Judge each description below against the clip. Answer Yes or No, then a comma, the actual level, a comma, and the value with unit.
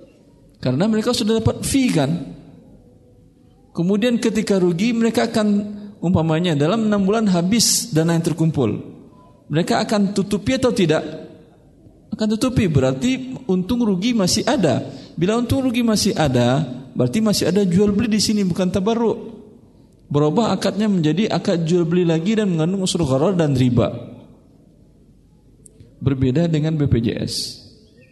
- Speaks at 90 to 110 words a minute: No, average, 130 wpm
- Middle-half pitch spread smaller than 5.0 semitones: No, wide, 5.6 semitones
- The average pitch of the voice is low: No, high, 190 Hz